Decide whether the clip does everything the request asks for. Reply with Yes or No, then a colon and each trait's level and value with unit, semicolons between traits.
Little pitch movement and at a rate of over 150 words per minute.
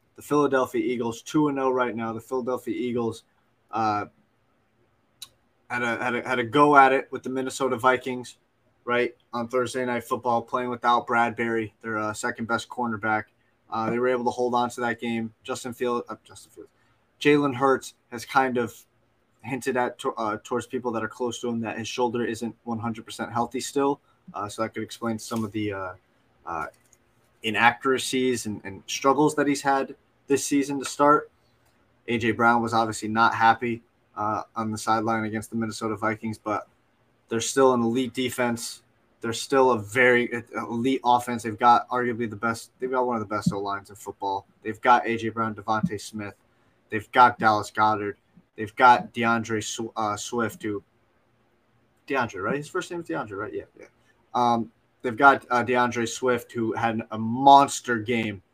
Yes: narrow, 2.0 semitones; average, 180 wpm